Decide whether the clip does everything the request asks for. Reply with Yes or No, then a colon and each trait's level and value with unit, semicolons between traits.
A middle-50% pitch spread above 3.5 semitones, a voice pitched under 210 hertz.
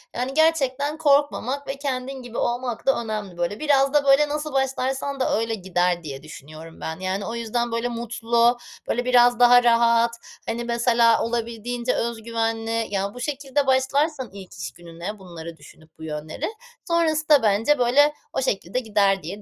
No: average, 4.6 semitones; high, 235 Hz